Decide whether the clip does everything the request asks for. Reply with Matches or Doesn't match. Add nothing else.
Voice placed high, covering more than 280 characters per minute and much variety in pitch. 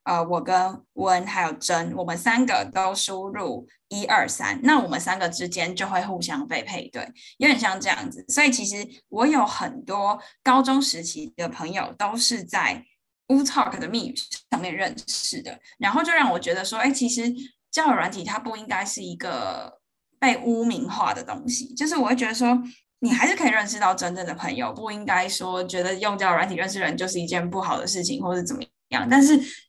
Matches